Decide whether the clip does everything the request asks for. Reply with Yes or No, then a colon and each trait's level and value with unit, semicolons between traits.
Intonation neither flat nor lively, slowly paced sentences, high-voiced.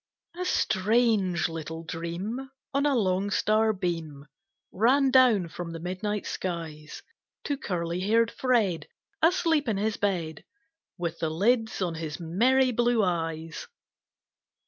No: wide, 6.0 semitones; slow, 125 wpm; high, 195 Hz